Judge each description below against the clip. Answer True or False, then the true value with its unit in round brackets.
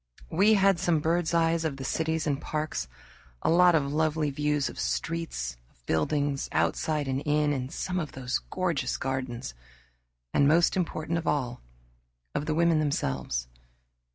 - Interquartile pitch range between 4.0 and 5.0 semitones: False (3.5 semitones)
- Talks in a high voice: False (150 Hz)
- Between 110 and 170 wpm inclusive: True (155 wpm)